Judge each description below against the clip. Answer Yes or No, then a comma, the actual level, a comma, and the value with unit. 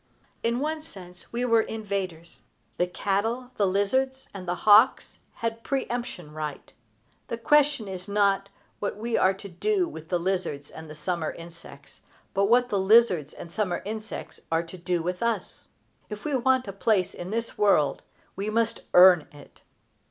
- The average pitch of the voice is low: No, high, 200 Hz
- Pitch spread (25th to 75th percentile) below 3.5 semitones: No, average, 4.7 semitones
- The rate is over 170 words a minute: No, average, 165 wpm